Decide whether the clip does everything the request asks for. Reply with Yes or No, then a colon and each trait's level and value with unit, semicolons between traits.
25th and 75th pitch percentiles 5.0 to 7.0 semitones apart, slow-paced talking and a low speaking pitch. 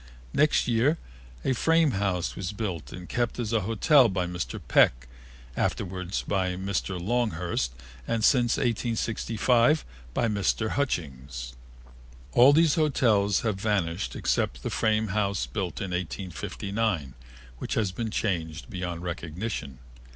No: average, 4.6 semitones; slow, 130 wpm; low, 100 Hz